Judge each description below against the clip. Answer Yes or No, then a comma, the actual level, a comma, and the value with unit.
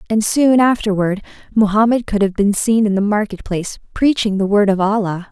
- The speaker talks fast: No, average, 190 wpm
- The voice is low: No, high, 210 Hz